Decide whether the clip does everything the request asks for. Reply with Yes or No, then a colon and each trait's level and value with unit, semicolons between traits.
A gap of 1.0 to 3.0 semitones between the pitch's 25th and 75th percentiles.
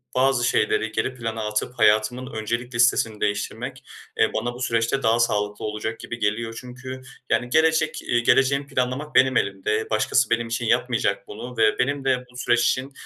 Yes: narrow, 2.6 semitones